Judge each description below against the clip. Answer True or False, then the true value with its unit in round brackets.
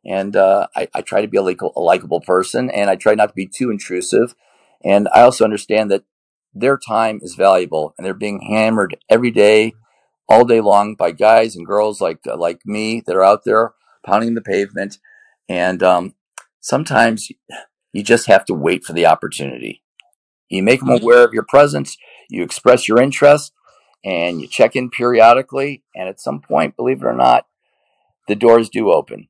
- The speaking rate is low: False (190 wpm)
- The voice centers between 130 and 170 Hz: False (105 Hz)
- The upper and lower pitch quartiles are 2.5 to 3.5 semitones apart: False (4.0 semitones)